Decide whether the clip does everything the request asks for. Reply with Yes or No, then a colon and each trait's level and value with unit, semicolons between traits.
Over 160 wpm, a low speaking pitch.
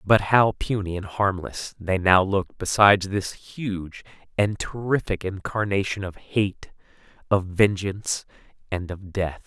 No: slow, 135 wpm; low, 100 Hz